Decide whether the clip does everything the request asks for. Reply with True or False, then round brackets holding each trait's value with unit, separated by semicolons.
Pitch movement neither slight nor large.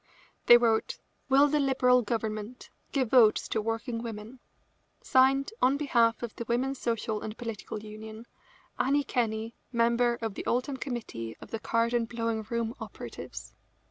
False (2.3 semitones)